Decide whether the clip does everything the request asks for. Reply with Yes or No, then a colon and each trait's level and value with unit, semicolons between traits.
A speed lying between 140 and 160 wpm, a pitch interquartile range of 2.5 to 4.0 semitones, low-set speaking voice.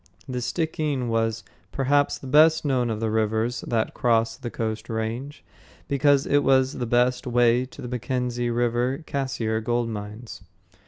Yes: average, 155 wpm; average, 2.8 semitones; low, 120 Hz